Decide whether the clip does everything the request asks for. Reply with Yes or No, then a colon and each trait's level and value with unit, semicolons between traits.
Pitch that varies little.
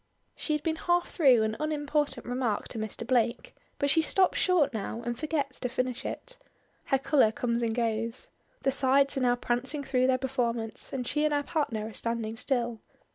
No: average, 3.7 semitones